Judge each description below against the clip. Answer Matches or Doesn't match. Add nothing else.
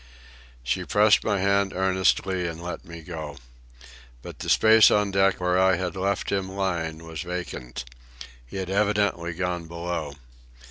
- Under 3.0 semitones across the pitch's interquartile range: Matches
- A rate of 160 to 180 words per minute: Doesn't match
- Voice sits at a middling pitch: Doesn't match